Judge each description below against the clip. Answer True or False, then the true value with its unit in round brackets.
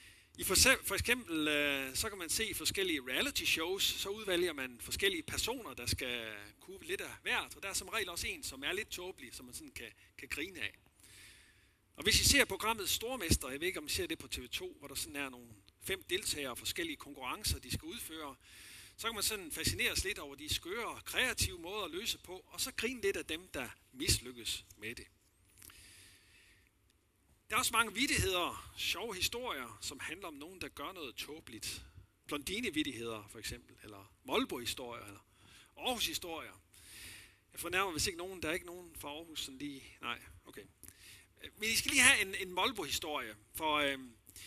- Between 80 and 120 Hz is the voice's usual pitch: False (130 Hz)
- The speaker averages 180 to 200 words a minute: True (195 wpm)